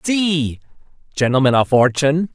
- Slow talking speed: Yes, slow, 100 wpm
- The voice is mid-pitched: Yes, medium, 145 Hz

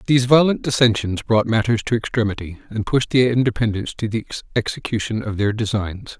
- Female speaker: No, male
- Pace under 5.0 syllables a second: No, 5.7 syllables/s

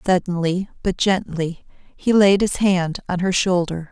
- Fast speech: No, average, 155 wpm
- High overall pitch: No, medium, 180 Hz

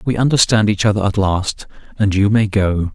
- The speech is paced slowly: No, fast, 205 wpm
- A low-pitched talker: Yes, low, 105 Hz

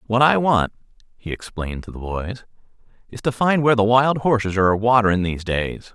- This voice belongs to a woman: No, male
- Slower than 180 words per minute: No, average, 190 wpm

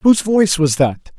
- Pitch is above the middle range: No, medium, 170 Hz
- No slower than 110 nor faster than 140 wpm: No, fast, 205 wpm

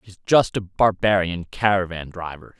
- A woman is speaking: No, male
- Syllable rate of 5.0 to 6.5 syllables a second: No, 4.6 syllables/s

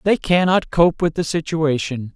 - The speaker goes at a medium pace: Yes, average, 165 wpm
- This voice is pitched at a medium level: Yes, medium, 160 Hz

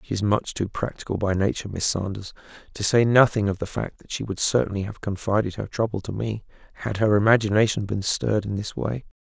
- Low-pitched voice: Yes, low, 105 Hz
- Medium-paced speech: No, fast, 210 wpm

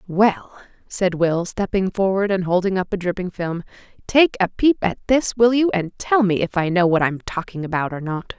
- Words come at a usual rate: No, fast, 215 wpm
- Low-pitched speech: No, high, 190 Hz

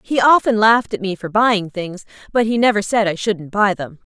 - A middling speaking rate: No, fast, 235 wpm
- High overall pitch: Yes, high, 205 Hz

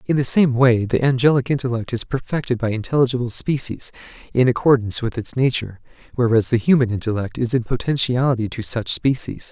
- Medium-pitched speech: No, low, 125 Hz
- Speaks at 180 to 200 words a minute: No, average, 170 wpm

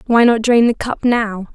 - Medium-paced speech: No, fast, 235 wpm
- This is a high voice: Yes, high, 230 Hz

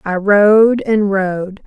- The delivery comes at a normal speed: Yes, average, 145 wpm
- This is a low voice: No, high, 200 Hz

